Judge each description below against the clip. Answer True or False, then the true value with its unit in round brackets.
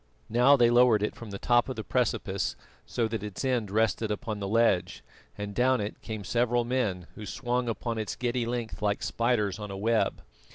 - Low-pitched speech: True (115 Hz)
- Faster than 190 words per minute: True (200 wpm)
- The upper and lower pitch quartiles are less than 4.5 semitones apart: True (2.8 semitones)